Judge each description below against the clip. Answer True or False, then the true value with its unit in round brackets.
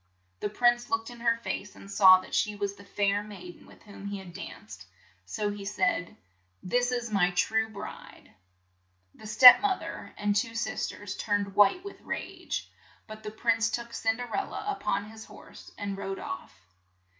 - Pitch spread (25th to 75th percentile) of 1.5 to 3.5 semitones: True (2.7 semitones)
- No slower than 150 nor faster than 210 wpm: True (205 wpm)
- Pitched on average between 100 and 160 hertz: False (205 Hz)